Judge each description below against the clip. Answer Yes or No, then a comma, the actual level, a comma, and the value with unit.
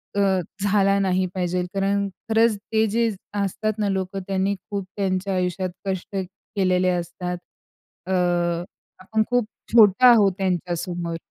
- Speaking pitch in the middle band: No, high, 195 Hz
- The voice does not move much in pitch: Yes, narrow, 1.9 semitones